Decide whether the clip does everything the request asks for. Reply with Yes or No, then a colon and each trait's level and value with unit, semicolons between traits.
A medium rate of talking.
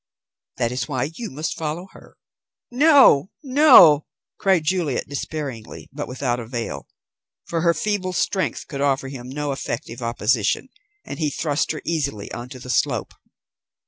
Yes: average, 145 wpm